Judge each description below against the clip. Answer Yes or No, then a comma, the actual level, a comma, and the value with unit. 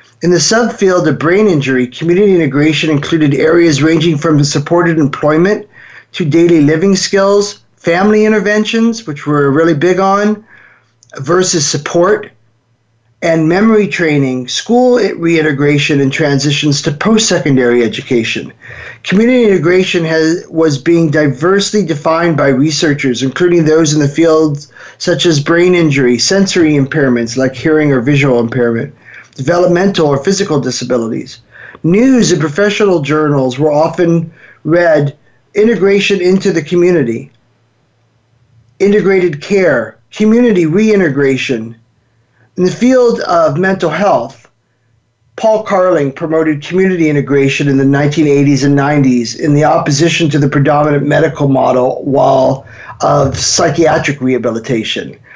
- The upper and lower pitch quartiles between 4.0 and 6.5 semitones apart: Yes, average, 4.7 semitones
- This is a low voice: No, medium, 155 Hz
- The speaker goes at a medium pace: No, slow, 120 wpm